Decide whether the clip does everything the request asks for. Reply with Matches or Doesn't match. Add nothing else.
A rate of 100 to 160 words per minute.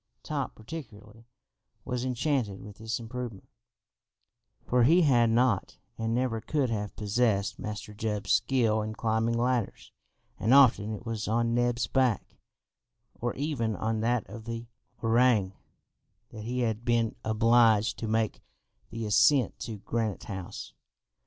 Matches